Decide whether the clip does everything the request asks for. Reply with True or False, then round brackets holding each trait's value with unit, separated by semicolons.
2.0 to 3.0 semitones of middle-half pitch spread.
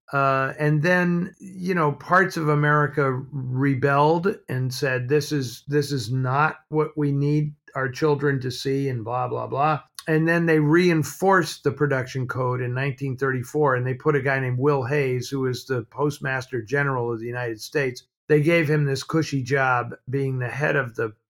True (2.7 semitones)